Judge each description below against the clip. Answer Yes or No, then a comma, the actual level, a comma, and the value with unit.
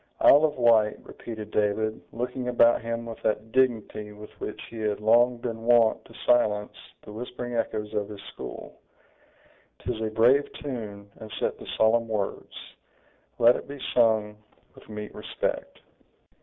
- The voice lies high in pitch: No, low, 115 Hz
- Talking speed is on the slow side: No, average, 155 wpm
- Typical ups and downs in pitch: No, narrow, 2.2 semitones